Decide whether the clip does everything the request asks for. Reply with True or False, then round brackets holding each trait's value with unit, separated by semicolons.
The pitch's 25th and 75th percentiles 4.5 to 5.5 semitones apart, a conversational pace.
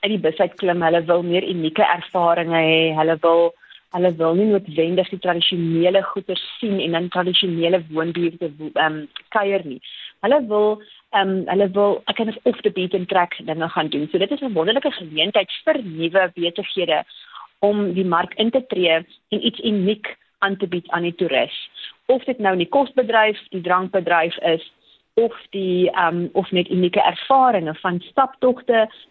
False (3.6 semitones; 180 wpm)